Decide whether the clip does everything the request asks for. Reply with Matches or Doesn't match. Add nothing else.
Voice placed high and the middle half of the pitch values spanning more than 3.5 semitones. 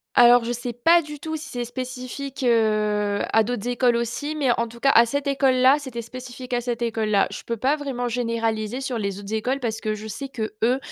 Doesn't match